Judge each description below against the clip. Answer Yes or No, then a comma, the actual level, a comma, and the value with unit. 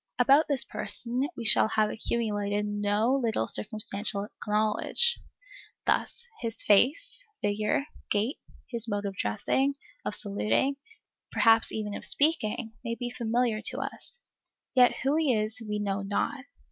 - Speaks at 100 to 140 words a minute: Yes, slow, 135 wpm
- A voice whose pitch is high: Yes, high, 225 Hz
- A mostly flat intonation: No, average, 4.0 semitones